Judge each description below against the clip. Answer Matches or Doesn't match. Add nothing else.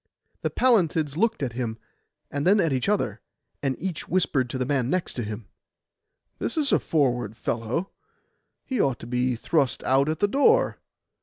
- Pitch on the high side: Doesn't match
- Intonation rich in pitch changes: Matches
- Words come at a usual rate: Matches